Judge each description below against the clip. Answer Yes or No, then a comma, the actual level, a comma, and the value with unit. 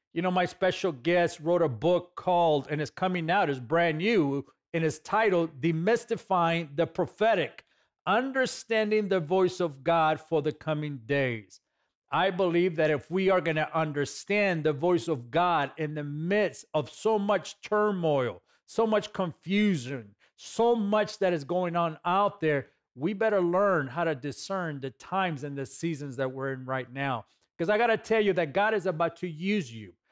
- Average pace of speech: Yes, average, 180 wpm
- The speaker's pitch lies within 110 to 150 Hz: No, medium, 170 Hz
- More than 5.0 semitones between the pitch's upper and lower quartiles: No, average, 4.3 semitones